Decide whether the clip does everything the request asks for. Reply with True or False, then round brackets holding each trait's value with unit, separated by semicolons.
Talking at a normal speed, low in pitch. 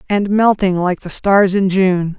False (195 wpm; 190 Hz)